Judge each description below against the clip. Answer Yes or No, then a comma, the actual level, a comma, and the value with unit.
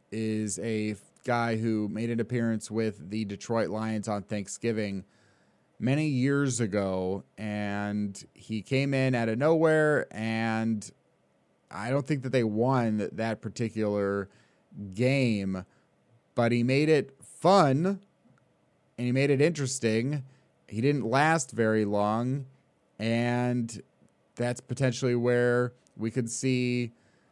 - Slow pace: Yes, slow, 120 wpm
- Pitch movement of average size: Yes, average, 3.4 semitones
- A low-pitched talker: Yes, low, 115 Hz